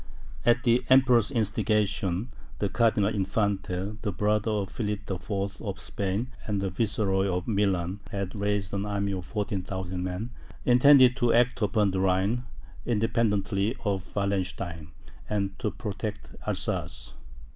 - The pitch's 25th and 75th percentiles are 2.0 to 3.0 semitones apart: Yes, narrow, 2.6 semitones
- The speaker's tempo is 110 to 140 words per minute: Yes, slow, 135 wpm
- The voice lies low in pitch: Yes, low, 100 Hz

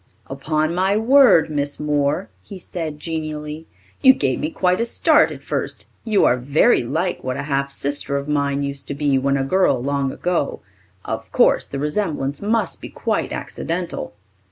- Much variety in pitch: No, average, 4.2 semitones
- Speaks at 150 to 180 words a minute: Yes, average, 175 wpm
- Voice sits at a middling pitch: Yes, medium, 150 Hz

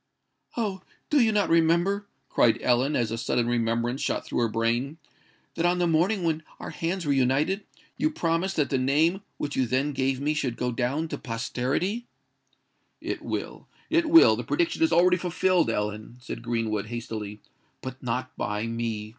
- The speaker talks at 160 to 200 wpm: Yes, average, 170 wpm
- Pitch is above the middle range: No, low, 135 Hz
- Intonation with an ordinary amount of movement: No, wide, 7.0 semitones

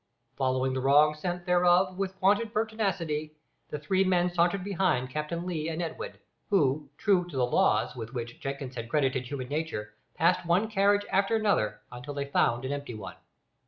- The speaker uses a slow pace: No, average, 175 wpm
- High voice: No, medium, 160 Hz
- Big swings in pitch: Yes, wide, 5.9 semitones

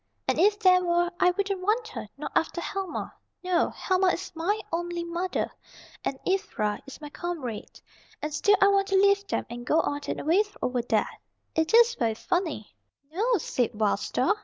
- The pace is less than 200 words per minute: Yes, average, 185 wpm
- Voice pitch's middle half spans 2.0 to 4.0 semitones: No, average, 4.8 semitones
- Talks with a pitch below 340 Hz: No, very high, 350 Hz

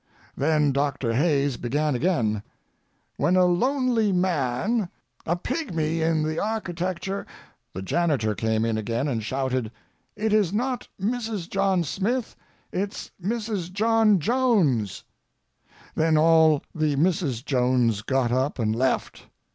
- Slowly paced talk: Yes, slow, 125 wpm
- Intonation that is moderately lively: No, wide, 7.4 semitones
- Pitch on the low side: No, medium, 160 Hz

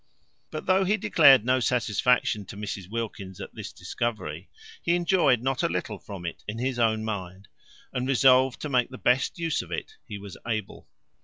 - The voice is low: Yes, low, 120 Hz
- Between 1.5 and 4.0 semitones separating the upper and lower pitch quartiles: No, average, 4.4 semitones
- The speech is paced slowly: No, average, 185 wpm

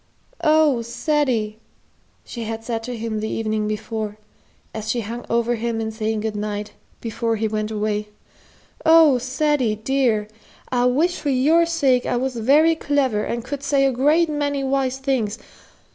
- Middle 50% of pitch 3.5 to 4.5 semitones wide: Yes, average, 4.1 semitones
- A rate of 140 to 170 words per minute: Yes, average, 160 wpm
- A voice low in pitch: No, high, 240 Hz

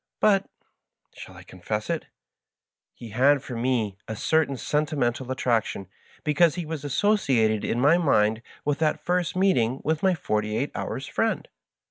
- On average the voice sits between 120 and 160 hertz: Yes, low, 135 Hz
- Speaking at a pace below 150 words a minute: No, average, 160 wpm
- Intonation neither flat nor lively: No, wide, 6.1 semitones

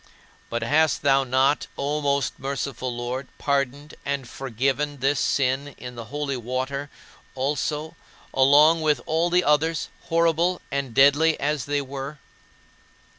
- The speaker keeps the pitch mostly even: Yes, narrow, 2.1 semitones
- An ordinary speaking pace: No, slow, 130 wpm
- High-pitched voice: No, medium, 140 Hz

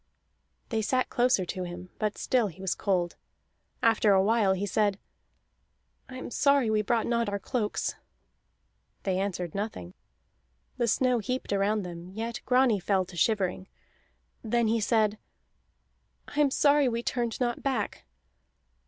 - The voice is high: Yes, high, 215 Hz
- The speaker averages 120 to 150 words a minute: Yes, average, 145 wpm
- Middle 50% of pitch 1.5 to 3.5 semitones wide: No, average, 3.9 semitones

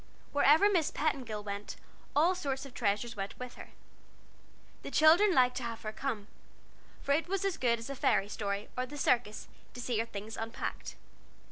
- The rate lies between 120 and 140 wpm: No, average, 180 wpm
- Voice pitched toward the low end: No, very high, 250 Hz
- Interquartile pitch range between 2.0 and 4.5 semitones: No, average, 5.2 semitones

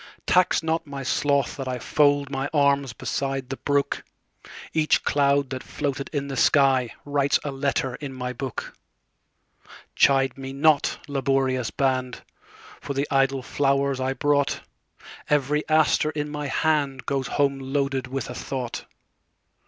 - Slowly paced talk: Yes, slow, 120 wpm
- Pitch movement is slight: Yes, narrow, 1.3 semitones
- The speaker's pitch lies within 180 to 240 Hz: No, medium, 140 Hz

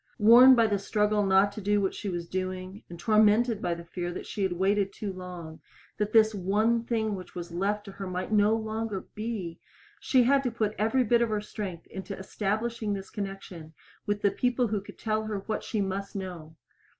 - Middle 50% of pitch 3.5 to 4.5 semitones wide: No, narrow, 2.5 semitones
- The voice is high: Yes, high, 205 Hz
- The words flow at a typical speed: No, fast, 210 wpm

